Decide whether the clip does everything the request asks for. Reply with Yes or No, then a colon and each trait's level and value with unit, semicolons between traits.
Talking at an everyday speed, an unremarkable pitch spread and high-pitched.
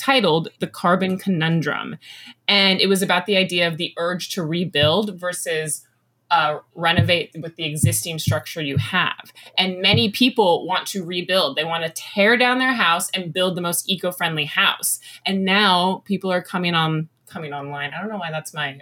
No: average, 180 wpm; average, 3.3 semitones; medium, 175 Hz